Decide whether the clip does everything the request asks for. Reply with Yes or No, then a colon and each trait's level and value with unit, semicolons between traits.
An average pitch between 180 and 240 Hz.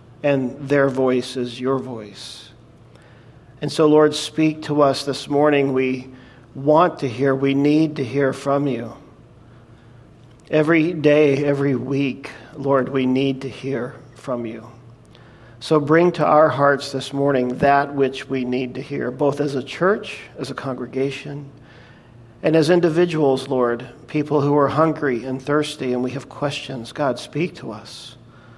No: low, 135 Hz